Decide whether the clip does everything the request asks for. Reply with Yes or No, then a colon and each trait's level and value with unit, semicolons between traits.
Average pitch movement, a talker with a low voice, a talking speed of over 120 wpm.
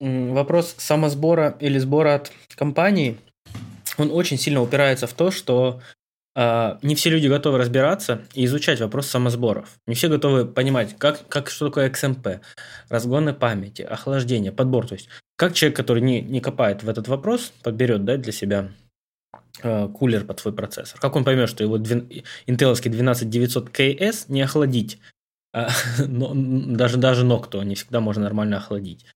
Yes: average, 3.5 semitones; low, 125 Hz; average, 155 wpm